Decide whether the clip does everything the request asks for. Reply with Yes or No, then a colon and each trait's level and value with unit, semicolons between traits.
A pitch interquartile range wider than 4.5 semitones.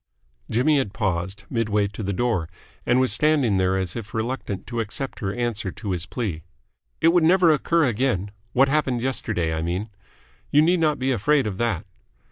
Yes: wide, 5.6 semitones